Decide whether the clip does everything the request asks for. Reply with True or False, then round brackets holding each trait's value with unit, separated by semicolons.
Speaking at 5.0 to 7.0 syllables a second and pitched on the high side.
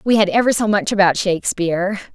True (6.4 syllables/s; 195 Hz)